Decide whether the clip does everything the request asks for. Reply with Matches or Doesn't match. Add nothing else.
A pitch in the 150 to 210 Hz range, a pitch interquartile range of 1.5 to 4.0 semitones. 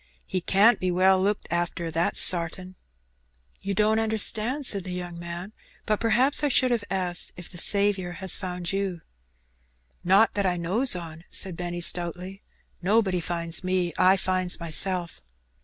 Matches